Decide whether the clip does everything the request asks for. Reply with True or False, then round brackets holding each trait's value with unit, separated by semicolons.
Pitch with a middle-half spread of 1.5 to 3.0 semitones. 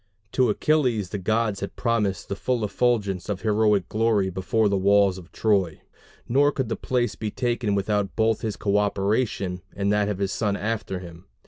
True (2.5 semitones)